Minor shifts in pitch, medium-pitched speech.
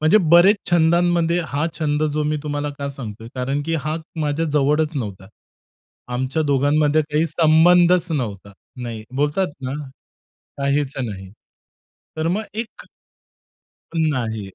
No: average, 3.7 semitones; medium, 150 Hz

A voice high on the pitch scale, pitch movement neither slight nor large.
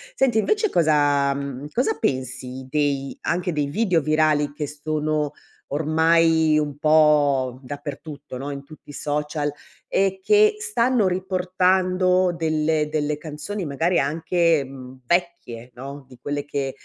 No: medium, 150 Hz; average, 3.7 semitones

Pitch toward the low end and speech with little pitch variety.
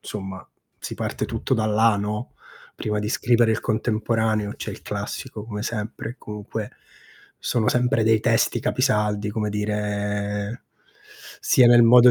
Yes: low, 110 Hz; narrow, 1.8 semitones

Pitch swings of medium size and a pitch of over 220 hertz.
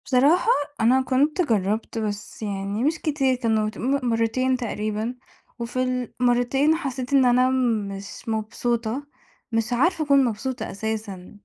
Yes: average, 3.4 semitones; high, 245 Hz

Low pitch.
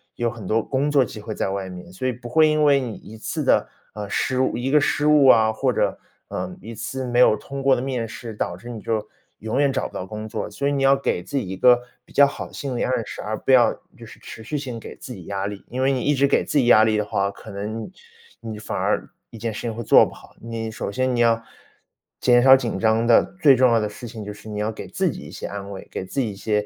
Yes: low, 115 Hz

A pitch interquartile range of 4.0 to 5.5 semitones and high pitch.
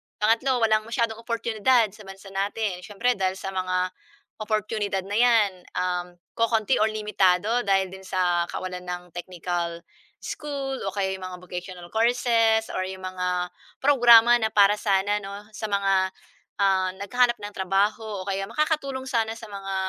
No: average, 3.3 semitones; high, 200 Hz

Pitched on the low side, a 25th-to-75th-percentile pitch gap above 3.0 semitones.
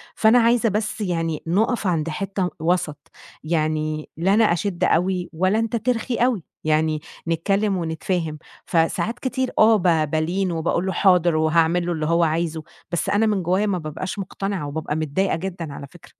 No: medium, 175 Hz; average, 3.9 semitones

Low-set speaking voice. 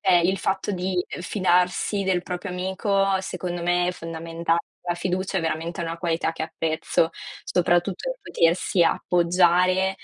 No: medium, 180 Hz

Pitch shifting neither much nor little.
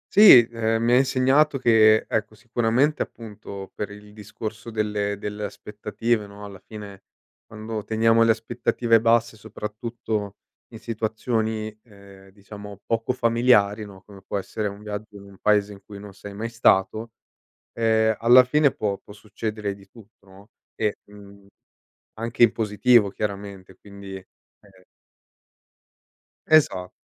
No: narrow, 2.1 semitones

